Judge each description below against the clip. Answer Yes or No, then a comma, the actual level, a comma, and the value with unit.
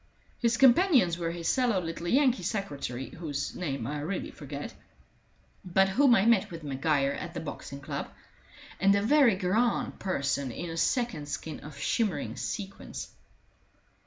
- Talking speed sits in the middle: Yes, average, 150 wpm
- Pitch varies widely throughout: Yes, wide, 7.4 semitones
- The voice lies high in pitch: No, medium, 175 Hz